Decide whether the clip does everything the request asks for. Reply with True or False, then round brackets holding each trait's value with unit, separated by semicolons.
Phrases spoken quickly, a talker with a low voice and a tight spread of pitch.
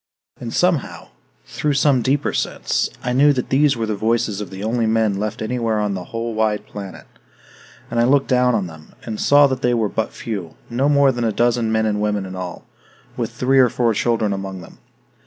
False (210 wpm; 115 Hz; 3.3 semitones)